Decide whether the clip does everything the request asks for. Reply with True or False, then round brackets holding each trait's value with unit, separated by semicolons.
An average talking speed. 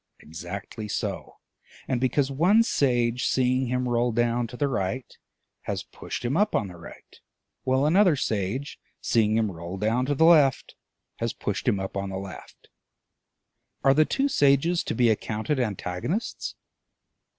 True (155 wpm)